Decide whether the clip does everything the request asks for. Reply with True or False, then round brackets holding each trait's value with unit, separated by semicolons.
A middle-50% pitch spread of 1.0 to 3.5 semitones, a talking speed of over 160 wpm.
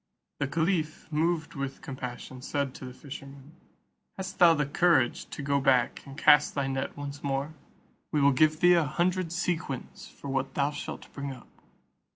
True (2.8 semitones; 175 wpm)